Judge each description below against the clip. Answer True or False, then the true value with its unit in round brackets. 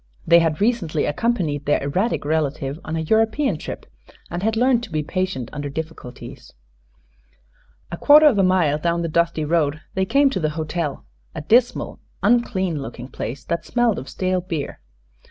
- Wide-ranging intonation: True (5.8 semitones)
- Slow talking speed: False (170 wpm)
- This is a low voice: False (170 Hz)